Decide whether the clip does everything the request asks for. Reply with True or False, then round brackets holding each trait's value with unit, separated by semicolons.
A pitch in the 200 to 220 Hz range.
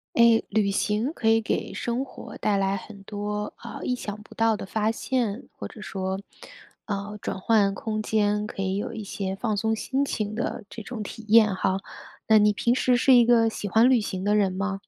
True (210 Hz)